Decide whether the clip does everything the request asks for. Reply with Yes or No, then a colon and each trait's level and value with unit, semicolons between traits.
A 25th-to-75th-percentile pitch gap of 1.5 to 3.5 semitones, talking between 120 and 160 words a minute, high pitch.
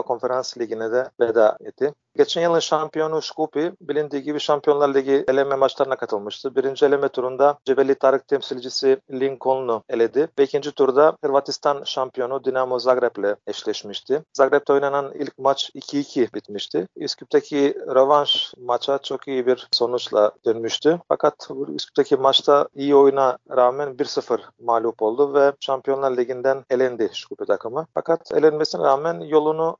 No: narrow, 2.6 semitones; average, 130 wpm; medium, 140 Hz